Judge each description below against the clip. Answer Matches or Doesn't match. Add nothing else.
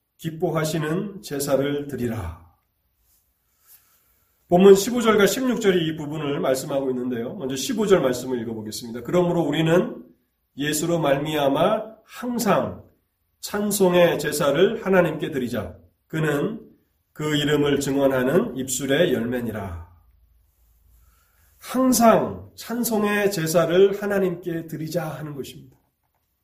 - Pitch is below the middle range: Doesn't match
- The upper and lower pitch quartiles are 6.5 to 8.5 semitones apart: Matches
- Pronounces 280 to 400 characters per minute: Doesn't match